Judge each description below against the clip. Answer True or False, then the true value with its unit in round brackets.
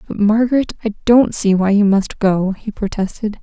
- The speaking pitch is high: True (210 Hz)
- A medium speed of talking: True (195 wpm)